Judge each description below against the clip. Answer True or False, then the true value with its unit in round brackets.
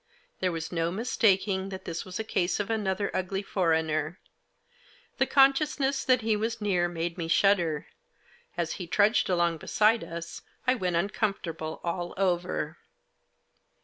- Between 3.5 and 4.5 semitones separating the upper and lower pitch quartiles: True (3.9 semitones)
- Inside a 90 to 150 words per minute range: True (145 wpm)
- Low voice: False (185 Hz)